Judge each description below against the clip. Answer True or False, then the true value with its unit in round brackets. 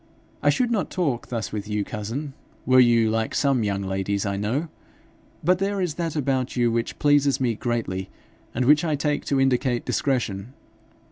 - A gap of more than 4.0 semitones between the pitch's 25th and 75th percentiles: True (5.1 semitones)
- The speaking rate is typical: True (180 wpm)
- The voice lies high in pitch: False (125 Hz)